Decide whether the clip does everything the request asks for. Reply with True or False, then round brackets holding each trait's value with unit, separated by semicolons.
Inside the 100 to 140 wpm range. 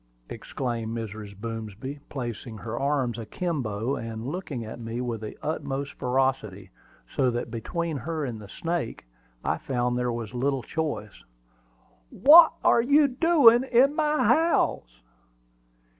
True (135 wpm)